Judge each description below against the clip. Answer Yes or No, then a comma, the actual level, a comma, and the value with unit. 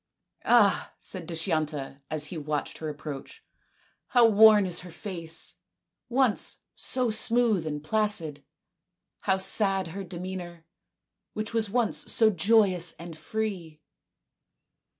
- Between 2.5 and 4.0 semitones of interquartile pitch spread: No, average, 5.2 semitones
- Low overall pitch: No, medium, 185 Hz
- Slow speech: Yes, slow, 125 wpm